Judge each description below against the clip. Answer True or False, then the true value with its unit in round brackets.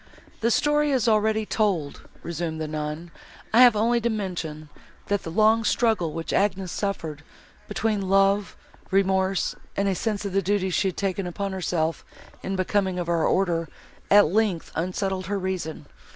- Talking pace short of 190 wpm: True (165 wpm)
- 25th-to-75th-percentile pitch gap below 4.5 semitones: True (3.4 semitones)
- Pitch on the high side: True (195 Hz)